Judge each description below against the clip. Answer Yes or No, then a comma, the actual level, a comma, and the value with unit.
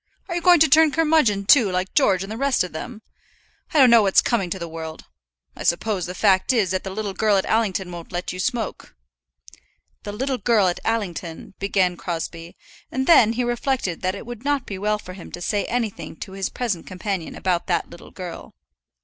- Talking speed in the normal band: No, fast, 210 wpm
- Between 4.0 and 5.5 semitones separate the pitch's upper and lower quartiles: Yes, average, 4.8 semitones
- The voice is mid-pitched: No, high, 200 Hz